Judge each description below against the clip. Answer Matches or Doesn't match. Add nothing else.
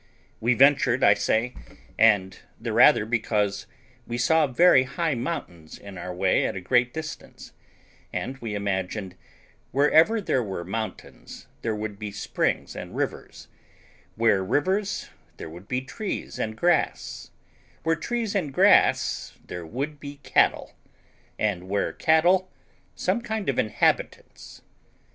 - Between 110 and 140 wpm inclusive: Matches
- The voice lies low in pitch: Matches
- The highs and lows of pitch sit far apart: Matches